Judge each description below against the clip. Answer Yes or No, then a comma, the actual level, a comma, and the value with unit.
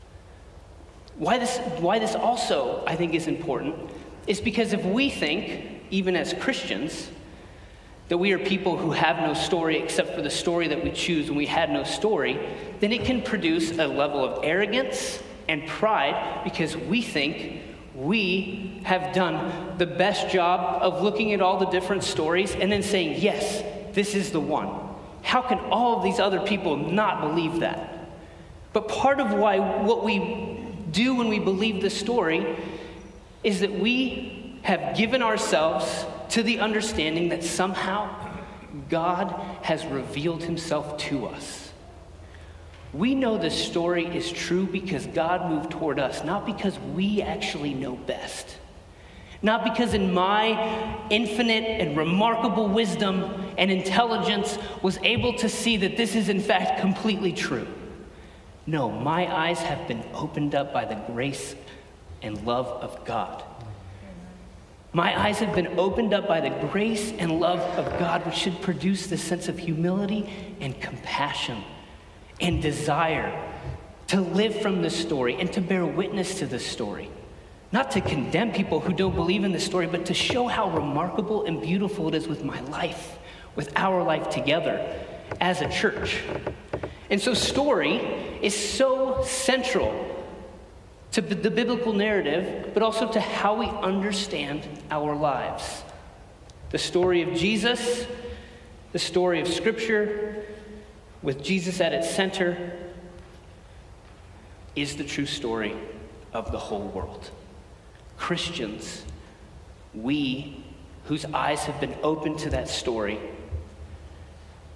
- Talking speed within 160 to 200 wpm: No, average, 145 wpm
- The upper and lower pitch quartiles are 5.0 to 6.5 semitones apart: Yes, wide, 5.6 semitones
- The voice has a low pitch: No, medium, 180 Hz